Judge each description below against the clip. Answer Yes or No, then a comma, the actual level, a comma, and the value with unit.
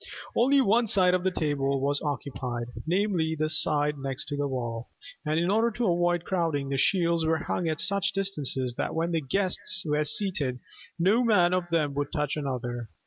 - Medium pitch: Yes, medium, 160 Hz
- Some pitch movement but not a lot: Yes, average, 4.6 semitones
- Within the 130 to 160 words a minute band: No, average, 190 wpm